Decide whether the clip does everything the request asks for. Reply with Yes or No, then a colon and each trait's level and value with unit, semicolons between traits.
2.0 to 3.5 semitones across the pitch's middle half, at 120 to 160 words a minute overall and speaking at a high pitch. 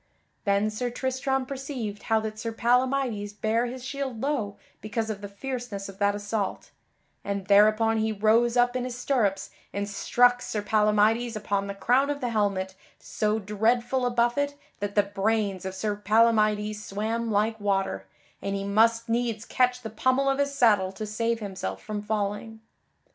No: average, 3.1 semitones; average, 170 wpm; high, 220 Hz